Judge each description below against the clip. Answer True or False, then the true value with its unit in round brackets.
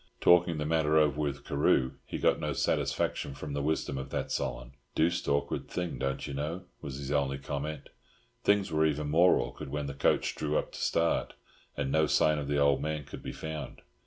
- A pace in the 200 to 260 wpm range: True (205 wpm)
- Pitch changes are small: True (1.9 semitones)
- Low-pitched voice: True (75 Hz)